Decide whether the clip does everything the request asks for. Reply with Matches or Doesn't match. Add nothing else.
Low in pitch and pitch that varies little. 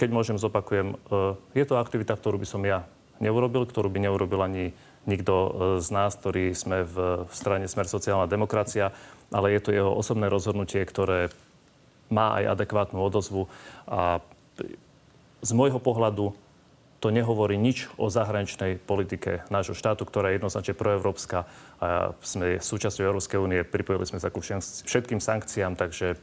Matches